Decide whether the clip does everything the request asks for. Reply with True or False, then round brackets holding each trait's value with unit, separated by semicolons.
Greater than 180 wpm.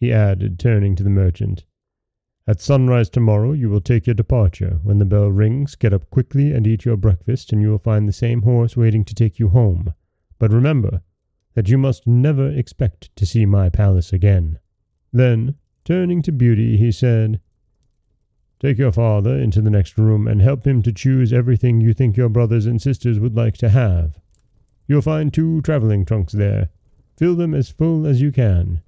True (190 wpm)